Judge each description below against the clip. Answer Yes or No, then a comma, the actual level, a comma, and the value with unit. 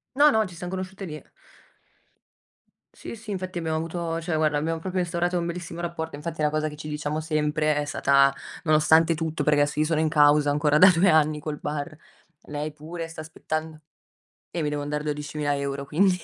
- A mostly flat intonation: Yes, narrow, 2.3 semitones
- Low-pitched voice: No, medium, 155 Hz